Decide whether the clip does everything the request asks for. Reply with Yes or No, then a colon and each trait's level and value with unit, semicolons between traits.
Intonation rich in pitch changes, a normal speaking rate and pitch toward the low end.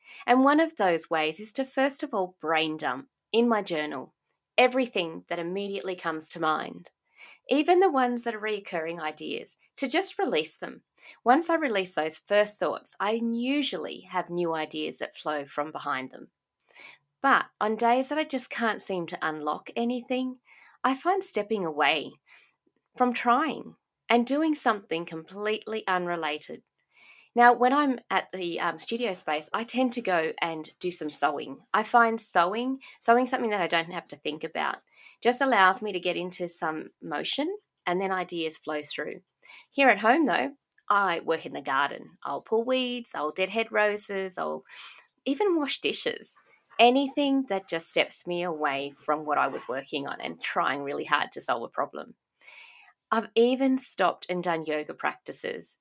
No: wide, 7.1 semitones; average, 170 wpm; high, 210 Hz